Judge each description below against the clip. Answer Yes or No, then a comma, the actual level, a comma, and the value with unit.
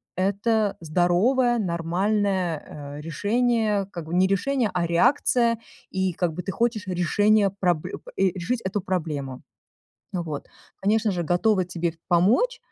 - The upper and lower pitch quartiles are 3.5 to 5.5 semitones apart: Yes, average, 4.0 semitones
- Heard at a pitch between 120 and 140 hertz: No, high, 190 Hz